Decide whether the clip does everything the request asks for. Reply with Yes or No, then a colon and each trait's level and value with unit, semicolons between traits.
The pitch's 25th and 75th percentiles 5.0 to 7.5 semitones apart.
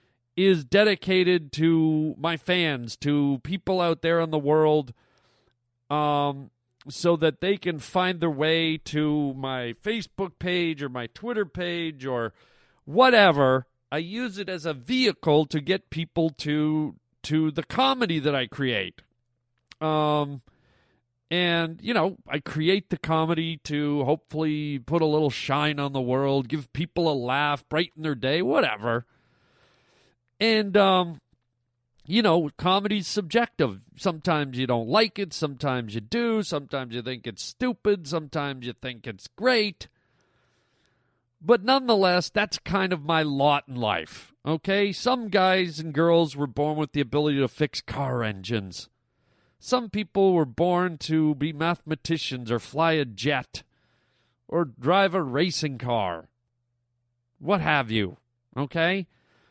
Yes: average, 5.3 semitones